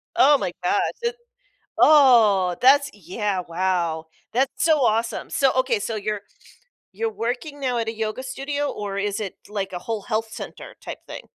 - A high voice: Yes, high, 225 Hz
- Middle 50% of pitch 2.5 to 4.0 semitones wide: No, average, 4.7 semitones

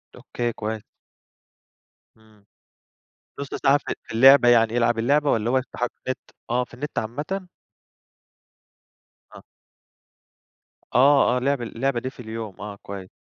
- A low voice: Yes, low, 120 Hz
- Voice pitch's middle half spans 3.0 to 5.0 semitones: Yes, average, 3.4 semitones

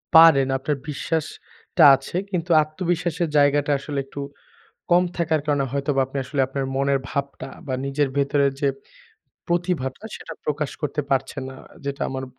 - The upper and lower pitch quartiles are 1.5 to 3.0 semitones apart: Yes, average, 2.7 semitones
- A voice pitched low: No, medium, 145 Hz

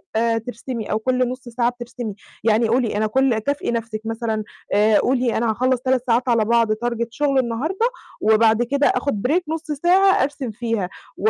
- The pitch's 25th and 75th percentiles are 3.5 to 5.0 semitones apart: No, average, 2.7 semitones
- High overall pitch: Yes, high, 235 Hz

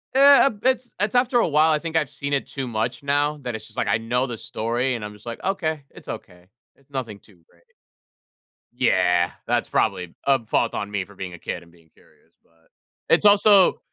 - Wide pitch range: Yes, wide, 7.4 semitones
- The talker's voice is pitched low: Yes, low, 130 Hz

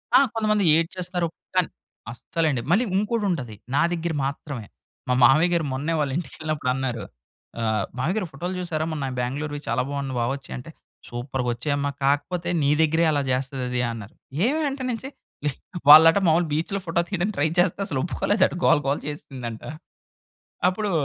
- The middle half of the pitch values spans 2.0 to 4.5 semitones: No, average, 4.9 semitones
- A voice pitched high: No, medium, 150 Hz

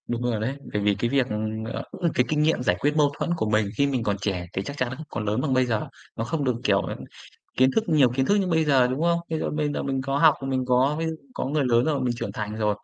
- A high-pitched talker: No, low, 130 Hz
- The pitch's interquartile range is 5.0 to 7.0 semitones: No, average, 4.5 semitones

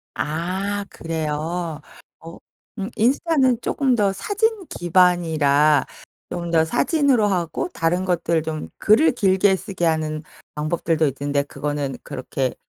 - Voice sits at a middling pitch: Yes, medium, 170 Hz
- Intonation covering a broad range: No, average, 4.7 semitones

